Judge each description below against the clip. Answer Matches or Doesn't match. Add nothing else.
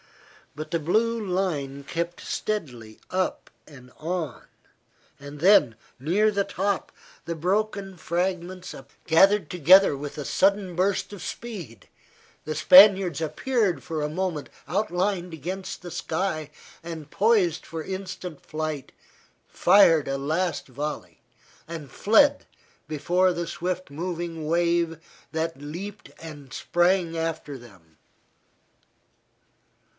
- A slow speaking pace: Matches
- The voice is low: Doesn't match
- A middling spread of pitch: Matches